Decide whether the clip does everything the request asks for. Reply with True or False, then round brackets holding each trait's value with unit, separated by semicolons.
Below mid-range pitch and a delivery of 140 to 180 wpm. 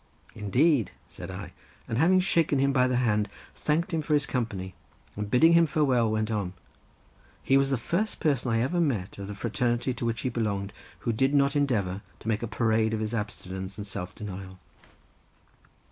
False (115 Hz; 190 wpm)